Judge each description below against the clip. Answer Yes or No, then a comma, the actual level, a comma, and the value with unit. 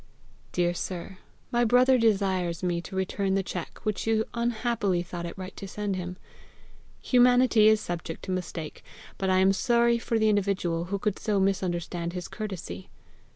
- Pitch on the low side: No, high, 195 Hz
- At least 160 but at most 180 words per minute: Yes, average, 165 wpm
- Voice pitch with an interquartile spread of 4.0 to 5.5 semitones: No, average, 3.5 semitones